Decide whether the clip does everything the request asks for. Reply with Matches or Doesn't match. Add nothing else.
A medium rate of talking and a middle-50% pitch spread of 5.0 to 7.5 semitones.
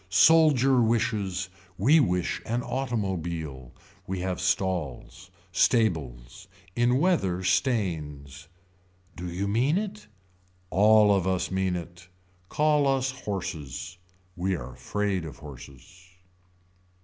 Doesn't match